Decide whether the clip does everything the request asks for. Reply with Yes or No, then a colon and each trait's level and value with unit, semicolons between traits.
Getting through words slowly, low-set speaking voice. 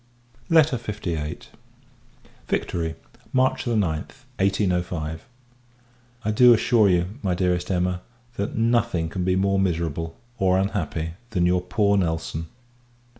Yes: slow, 115 wpm; very low, 90 Hz